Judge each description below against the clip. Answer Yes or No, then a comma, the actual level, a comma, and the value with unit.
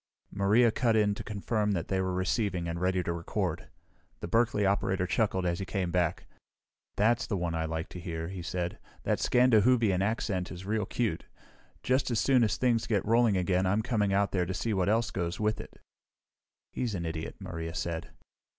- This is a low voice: Yes, very low, 95 Hz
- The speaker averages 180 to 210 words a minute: Yes, average, 195 wpm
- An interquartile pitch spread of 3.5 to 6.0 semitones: Yes, average, 3.8 semitones